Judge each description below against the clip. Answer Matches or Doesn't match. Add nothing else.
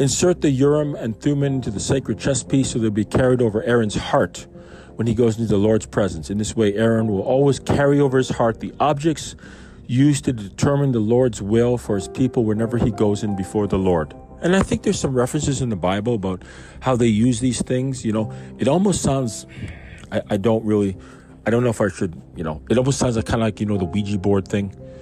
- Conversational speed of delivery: Doesn't match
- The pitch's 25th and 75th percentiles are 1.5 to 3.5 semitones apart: Doesn't match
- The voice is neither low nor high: Doesn't match